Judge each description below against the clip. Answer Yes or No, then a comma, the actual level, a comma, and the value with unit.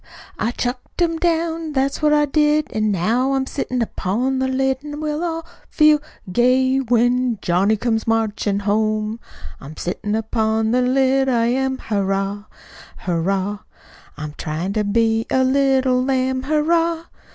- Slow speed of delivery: No, average, 145 wpm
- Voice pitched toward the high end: Yes, very high, 250 Hz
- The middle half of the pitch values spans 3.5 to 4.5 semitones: Yes, average, 4.1 semitones